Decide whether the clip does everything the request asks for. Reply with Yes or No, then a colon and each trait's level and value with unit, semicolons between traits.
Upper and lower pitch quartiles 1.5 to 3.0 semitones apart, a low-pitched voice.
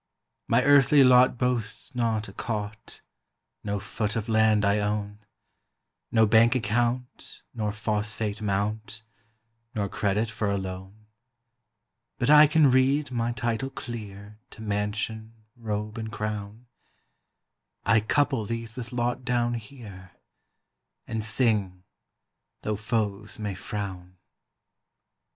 Yes: narrow, 2.6 semitones; low, 110 Hz